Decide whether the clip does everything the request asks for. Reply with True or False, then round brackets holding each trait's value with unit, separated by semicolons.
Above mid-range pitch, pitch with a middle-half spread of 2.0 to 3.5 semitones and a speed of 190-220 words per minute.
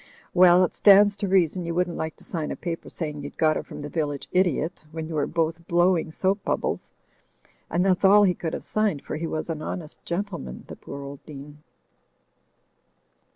False (165 Hz; 3.1 semitones; 200 wpm)